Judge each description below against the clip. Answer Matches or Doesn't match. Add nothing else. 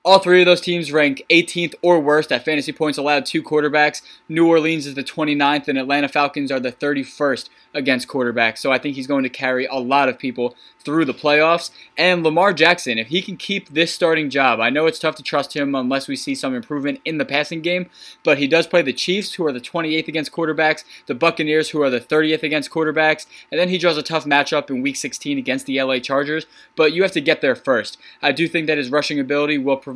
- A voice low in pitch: Doesn't match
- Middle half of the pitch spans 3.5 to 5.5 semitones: Doesn't match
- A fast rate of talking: Matches